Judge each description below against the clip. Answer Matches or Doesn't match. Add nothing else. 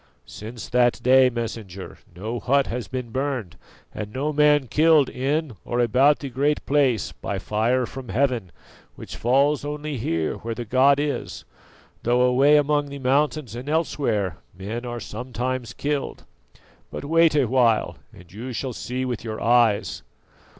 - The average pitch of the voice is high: Doesn't match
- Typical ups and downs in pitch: Matches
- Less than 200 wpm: Matches